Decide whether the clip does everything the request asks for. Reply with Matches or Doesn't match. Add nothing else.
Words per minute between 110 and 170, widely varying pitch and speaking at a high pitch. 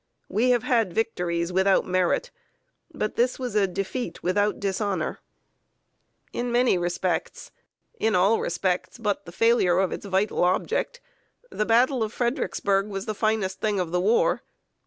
Doesn't match